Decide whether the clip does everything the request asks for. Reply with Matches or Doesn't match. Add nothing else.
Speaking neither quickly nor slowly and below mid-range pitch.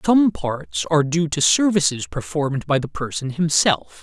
Doesn't match